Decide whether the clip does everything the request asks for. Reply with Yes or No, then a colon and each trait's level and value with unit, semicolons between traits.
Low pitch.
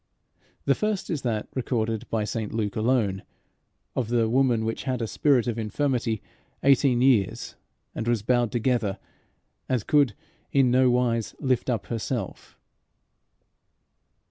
Yes: low, 120 Hz